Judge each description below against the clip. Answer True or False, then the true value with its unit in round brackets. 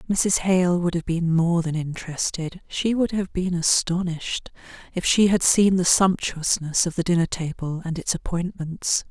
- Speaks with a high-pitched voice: False (175 Hz)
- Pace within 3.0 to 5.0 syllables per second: True (4.6 syllables/s)